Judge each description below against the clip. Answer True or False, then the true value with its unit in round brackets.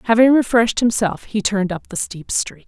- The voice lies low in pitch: False (215 Hz)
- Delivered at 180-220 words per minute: True (200 wpm)